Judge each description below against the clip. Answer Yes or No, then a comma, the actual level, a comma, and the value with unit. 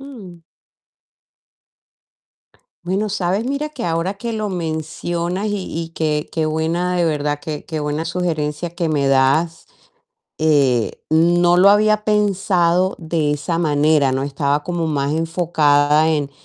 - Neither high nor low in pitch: Yes, medium, 165 Hz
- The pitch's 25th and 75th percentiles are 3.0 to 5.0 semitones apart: Yes, average, 3.3 semitones